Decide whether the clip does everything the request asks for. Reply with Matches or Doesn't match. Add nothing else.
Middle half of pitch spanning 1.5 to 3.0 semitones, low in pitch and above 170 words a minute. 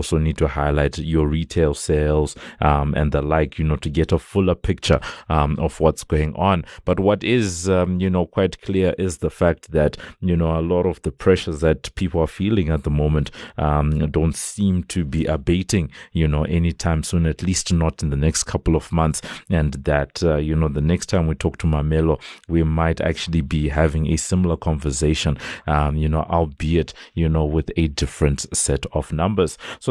Matches